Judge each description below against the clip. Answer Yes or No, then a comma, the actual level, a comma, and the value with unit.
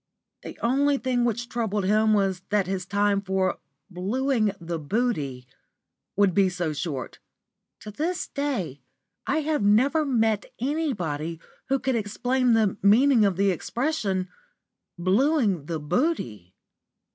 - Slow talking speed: Yes, slow, 130 wpm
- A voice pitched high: Yes, high, 210 Hz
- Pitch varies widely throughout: Yes, wide, 5.8 semitones